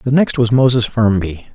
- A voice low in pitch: Yes, low, 120 Hz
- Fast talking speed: No, average, 195 wpm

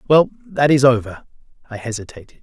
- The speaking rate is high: No, average, 150 wpm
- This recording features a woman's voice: No, male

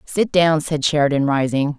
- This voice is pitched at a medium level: Yes, medium, 150 Hz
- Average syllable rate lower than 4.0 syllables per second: No, 4.7 syllables/s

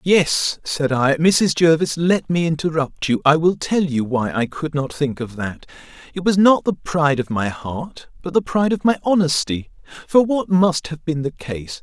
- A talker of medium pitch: Yes, medium, 160 Hz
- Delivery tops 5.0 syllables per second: No, 4.5 syllables/s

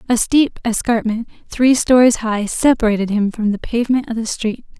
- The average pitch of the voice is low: No, high, 230 Hz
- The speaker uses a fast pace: No, average, 175 wpm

